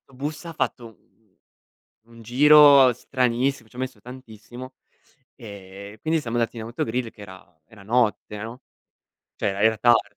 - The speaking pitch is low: Yes, low, 120 Hz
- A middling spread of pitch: Yes, average, 3.0 semitones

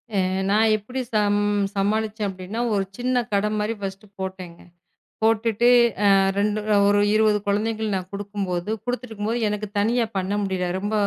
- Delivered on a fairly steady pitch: Yes, narrow, 1.8 semitones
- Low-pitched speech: No, high, 210 Hz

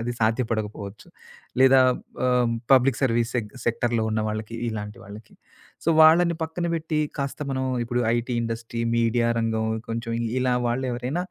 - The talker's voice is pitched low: Yes, low, 120 Hz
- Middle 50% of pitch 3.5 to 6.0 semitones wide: No, narrow, 2.6 semitones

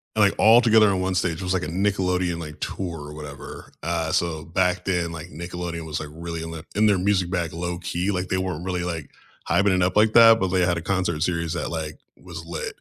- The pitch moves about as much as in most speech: No, narrow, 2.2 semitones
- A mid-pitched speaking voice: No, very low, 90 Hz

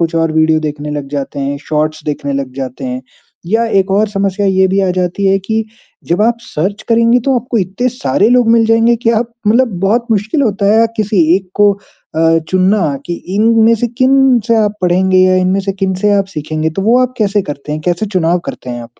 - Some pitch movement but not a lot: No, wide, 5.8 semitones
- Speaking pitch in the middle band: No, high, 195 Hz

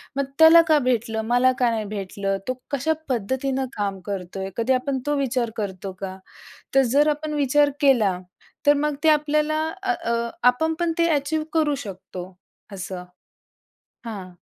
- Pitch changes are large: Yes, wide, 6.5 semitones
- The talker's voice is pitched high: Yes, very high, 255 Hz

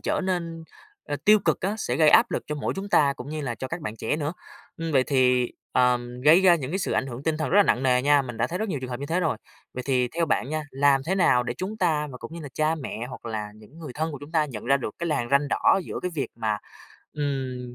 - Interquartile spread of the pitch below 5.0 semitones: Yes, average, 4.6 semitones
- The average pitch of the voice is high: No, medium, 145 Hz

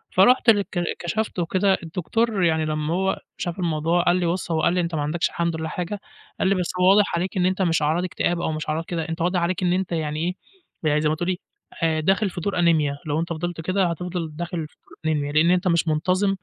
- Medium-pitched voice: Yes, medium, 175 Hz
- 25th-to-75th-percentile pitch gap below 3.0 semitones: Yes, narrow, 2.5 semitones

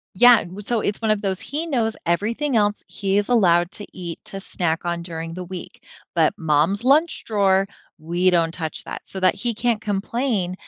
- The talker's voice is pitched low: No, high, 195 Hz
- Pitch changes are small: No, average, 4.3 semitones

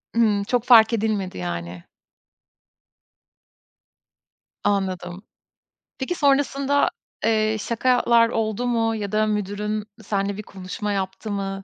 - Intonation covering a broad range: No, average, 2.8 semitones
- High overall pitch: Yes, high, 215 Hz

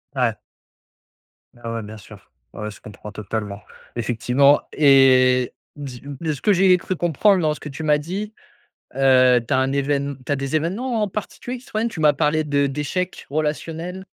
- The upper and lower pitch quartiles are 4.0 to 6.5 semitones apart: Yes, average, 4.7 semitones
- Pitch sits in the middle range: Yes, medium, 145 Hz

